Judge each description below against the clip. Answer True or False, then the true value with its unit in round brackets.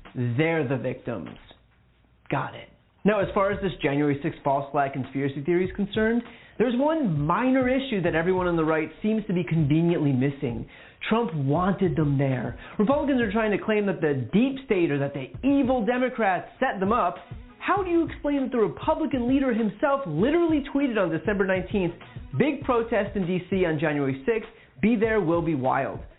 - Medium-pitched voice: False (195 Hz)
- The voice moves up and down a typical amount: False (7.2 semitones)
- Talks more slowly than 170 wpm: False (180 wpm)